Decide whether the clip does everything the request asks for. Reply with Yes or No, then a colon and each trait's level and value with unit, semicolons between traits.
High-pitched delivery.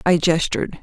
No: medium, 170 Hz